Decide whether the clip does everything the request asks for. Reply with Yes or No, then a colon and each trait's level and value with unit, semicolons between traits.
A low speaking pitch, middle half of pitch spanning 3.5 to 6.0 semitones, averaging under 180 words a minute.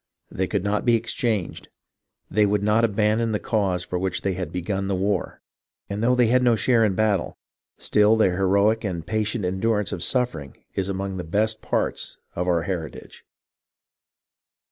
No: low, 100 Hz; average, 2.8 semitones; average, 170 wpm